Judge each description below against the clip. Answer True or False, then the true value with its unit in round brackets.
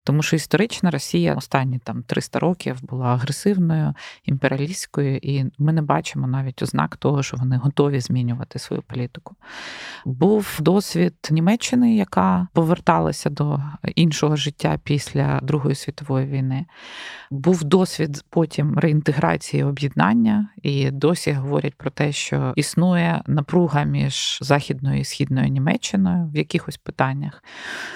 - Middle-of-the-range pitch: True (150 Hz)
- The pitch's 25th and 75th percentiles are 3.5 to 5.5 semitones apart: True (3.8 semitones)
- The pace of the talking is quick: False (120 wpm)